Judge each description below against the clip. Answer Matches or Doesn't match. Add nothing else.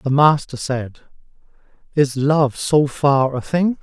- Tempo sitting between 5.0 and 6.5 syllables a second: Doesn't match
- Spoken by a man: Matches